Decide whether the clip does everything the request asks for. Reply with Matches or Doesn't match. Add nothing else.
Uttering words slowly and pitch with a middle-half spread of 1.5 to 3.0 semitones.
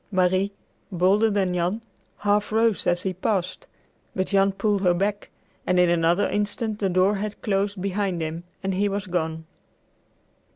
Doesn't match